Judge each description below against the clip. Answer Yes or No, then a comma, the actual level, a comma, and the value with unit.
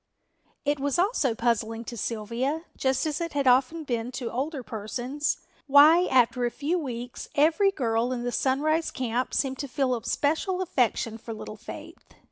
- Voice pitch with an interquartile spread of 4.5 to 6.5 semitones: No, average, 3.9 semitones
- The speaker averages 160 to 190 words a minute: Yes, average, 170 wpm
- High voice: Yes, very high, 260 Hz